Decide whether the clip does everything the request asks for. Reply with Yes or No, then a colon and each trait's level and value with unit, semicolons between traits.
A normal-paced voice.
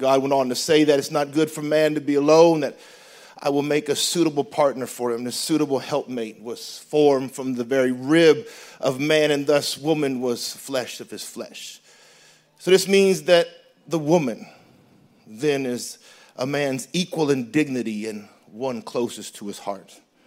Yes: average, 180 wpm